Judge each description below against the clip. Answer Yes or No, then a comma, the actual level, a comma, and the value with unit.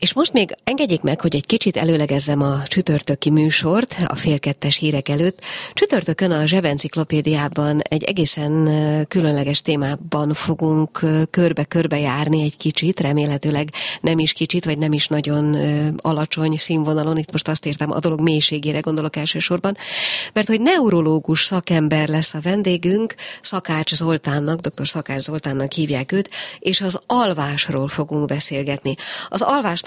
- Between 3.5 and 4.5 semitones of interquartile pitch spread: No, narrow, 2.5 semitones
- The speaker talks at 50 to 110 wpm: No, average, 135 wpm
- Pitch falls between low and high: Yes, medium, 155 Hz